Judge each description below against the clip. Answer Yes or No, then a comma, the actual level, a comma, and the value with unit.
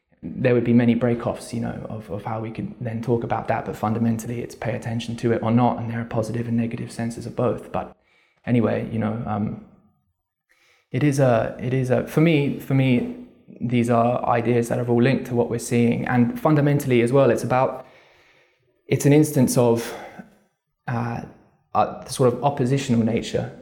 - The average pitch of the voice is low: Yes, low, 120 Hz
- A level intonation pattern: Yes, narrow, 1.9 semitones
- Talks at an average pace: Yes, average, 195 wpm